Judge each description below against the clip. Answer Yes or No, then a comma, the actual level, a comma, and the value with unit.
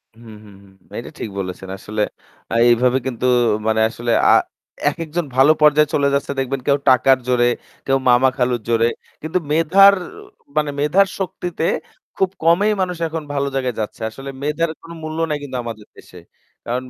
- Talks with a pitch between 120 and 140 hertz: Yes, low, 135 Hz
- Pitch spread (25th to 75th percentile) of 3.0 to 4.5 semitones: No, average, 4.9 semitones